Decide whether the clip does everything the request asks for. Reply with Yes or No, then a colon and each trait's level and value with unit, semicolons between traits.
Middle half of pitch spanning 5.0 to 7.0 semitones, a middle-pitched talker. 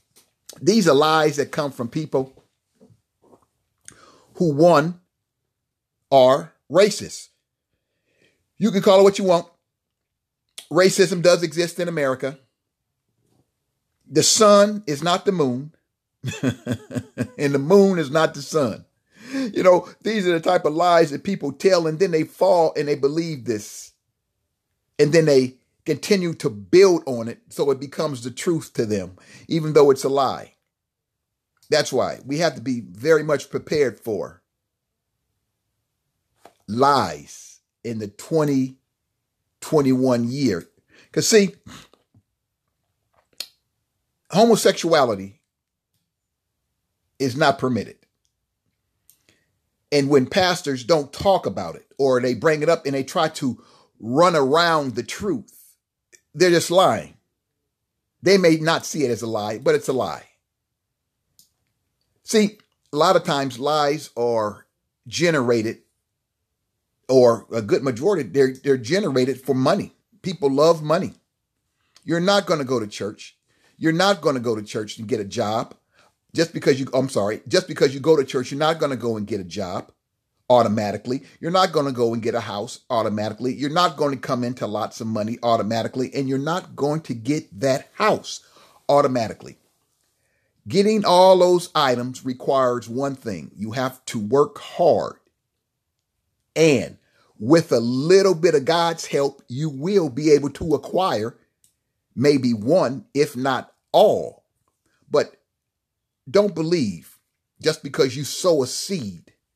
Yes: wide, 5.5 semitones; medium, 145 Hz